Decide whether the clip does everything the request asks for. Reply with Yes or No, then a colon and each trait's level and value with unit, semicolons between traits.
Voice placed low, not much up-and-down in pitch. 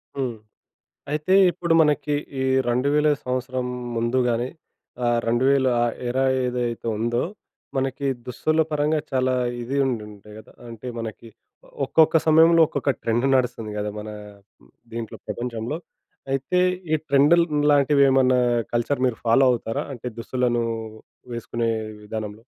No: low, 125 Hz; average, 3.2 semitones